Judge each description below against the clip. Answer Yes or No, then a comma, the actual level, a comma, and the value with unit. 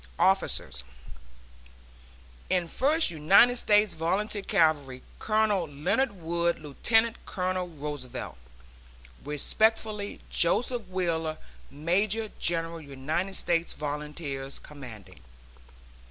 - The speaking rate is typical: No, slow, 80 wpm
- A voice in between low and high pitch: Yes, medium, 170 Hz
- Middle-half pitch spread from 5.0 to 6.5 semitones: Yes, wide, 5.5 semitones